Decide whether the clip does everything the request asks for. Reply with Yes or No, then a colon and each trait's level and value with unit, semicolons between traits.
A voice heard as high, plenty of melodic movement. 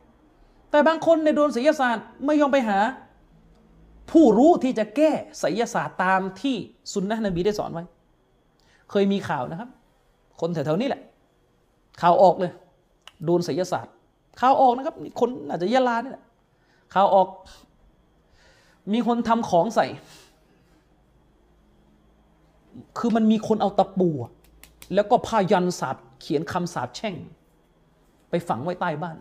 Yes: high, 200 Hz; wide, 5.8 semitones